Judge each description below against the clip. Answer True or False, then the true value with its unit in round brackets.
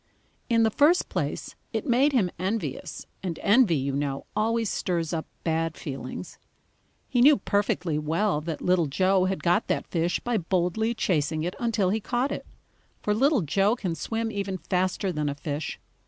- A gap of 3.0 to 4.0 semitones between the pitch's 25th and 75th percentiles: False (5.4 semitones)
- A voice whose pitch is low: False (185 Hz)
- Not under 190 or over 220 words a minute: False (170 wpm)